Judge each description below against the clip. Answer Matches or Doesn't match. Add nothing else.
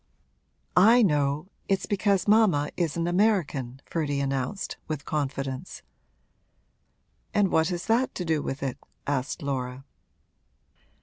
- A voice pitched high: Doesn't match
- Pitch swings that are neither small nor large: Doesn't match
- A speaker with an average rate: Doesn't match